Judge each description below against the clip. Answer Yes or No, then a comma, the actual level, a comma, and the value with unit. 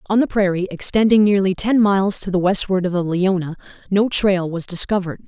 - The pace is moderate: Yes, average, 195 wpm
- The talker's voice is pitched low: No, high, 190 Hz